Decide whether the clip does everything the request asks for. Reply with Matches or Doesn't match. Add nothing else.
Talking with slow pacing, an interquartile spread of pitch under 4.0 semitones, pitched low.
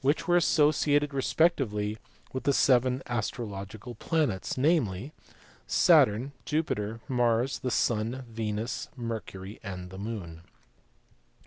Doesn't match